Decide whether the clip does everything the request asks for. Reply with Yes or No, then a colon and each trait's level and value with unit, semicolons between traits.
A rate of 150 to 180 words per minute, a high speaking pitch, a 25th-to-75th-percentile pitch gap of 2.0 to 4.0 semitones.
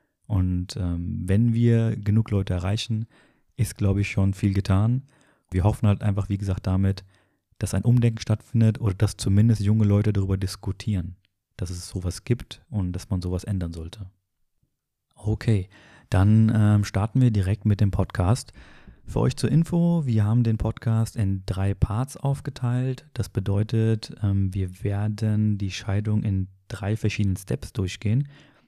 No: average, 155 wpm; low, 105 Hz; average, 2.8 semitones